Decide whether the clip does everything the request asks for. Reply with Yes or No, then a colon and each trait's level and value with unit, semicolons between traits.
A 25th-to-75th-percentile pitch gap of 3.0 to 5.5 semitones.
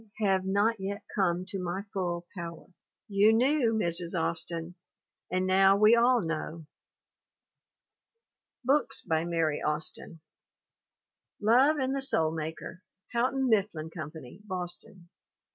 Yes: average, 4.9 semitones